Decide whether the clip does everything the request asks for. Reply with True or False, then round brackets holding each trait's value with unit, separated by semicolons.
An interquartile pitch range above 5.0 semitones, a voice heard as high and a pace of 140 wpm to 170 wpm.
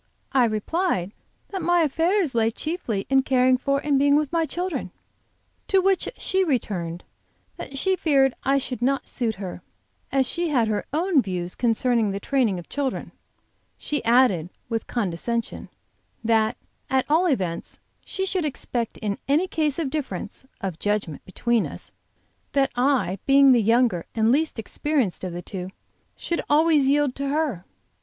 True (5.6 semitones; 260 Hz; 160 wpm)